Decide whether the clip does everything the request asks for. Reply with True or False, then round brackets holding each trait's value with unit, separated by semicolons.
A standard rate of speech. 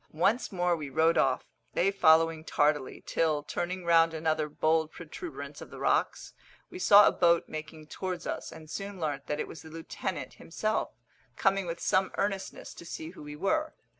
True (180 wpm)